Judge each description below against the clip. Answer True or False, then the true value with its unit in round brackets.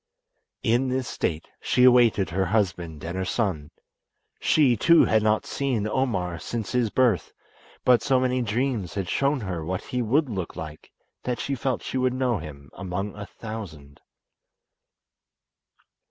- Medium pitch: False (110 Hz)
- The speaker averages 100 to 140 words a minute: False (155 wpm)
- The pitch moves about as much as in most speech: False (5.9 semitones)